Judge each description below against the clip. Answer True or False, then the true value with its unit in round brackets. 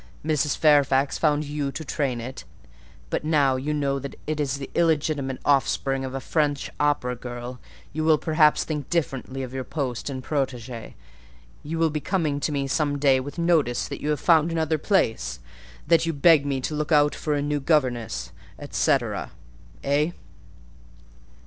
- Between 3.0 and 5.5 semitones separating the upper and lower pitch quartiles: False (2.6 semitones)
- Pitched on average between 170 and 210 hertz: False (145 Hz)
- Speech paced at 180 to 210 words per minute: False (165 wpm)